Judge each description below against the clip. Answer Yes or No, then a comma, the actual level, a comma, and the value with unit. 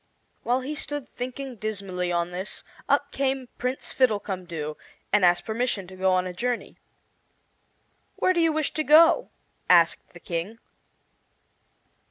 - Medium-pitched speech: No, high, 220 Hz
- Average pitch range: No, wide, 6.7 semitones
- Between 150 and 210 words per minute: No, average, 140 wpm